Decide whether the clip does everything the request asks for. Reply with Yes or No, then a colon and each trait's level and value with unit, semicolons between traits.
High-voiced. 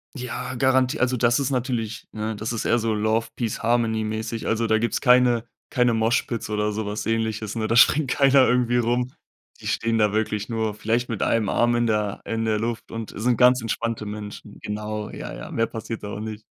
No: low, 115 Hz